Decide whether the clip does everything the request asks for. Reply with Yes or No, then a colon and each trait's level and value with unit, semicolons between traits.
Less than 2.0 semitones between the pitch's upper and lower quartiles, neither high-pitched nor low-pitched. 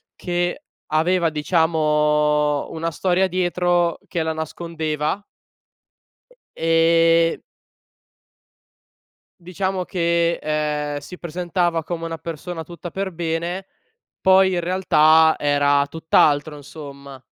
No: narrow, 2.5 semitones; medium, 165 Hz